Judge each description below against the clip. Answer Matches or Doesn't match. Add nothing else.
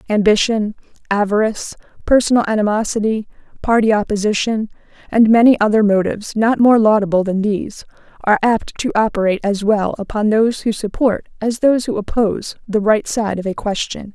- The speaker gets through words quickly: Doesn't match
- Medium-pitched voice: Doesn't match